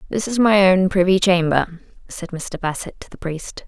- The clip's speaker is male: No, female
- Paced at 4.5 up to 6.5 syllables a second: Yes, 4.7 syllables/s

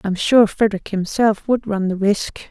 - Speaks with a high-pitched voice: Yes, high, 205 Hz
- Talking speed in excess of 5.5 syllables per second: No, 4.6 syllables/s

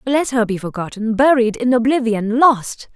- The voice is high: Yes, high, 235 Hz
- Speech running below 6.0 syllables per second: Yes, 4.6 syllables/s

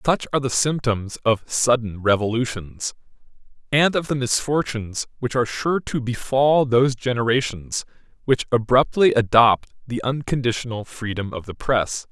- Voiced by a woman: No, male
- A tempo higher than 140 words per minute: No, slow, 135 wpm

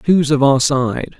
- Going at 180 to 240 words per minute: Yes, average, 200 wpm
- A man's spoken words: Yes, male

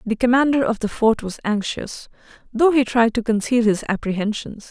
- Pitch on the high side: Yes, high, 230 Hz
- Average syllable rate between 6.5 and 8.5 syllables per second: No, 5.1 syllables/s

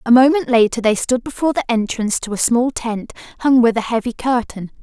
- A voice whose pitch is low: No, high, 240 Hz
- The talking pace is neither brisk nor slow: No, fast, 210 wpm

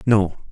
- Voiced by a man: Yes, male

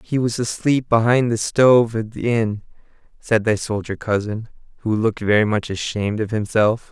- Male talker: Yes, male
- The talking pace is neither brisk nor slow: Yes, average, 175 wpm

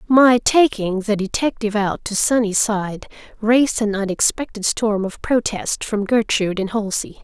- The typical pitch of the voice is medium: No, high, 215 Hz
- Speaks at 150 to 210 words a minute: No, average, 140 wpm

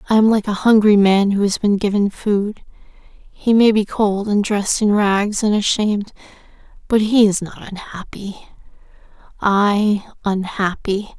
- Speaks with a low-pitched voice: No, high, 205 Hz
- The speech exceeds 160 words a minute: No, average, 150 wpm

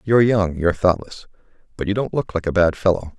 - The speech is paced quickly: Yes, fast, 225 wpm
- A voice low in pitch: Yes, very low, 95 Hz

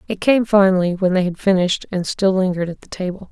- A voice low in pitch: No, high, 190 Hz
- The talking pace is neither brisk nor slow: No, fast, 235 wpm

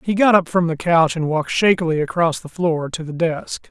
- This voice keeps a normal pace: No, fast, 245 wpm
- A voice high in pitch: No, medium, 165 Hz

